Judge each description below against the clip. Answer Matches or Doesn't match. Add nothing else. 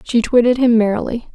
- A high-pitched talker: Matches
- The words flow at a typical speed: Matches